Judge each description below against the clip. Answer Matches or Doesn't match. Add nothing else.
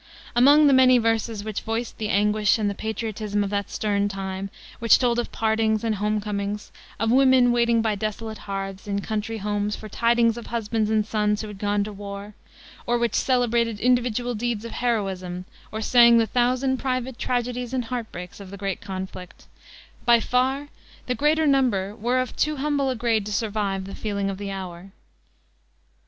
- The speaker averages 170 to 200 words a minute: Matches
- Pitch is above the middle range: Matches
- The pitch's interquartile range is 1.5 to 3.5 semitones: Matches